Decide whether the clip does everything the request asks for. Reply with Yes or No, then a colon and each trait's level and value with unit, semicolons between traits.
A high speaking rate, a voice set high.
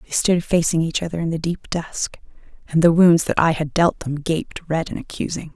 No: fast, 225 wpm; medium, 165 Hz